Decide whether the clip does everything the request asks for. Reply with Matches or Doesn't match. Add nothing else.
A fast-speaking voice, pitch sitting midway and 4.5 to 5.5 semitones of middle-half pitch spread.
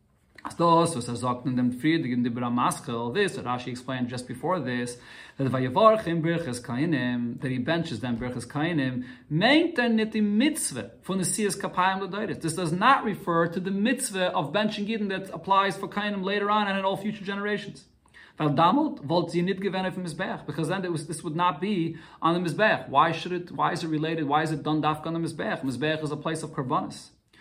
Doesn't match